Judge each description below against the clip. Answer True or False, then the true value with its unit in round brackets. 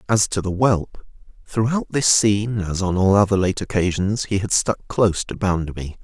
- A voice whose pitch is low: True (100 Hz)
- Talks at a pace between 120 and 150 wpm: False (190 wpm)